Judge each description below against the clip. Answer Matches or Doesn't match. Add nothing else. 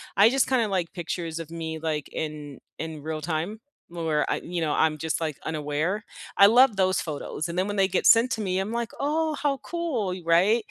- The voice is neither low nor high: Matches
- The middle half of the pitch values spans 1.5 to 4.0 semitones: Doesn't match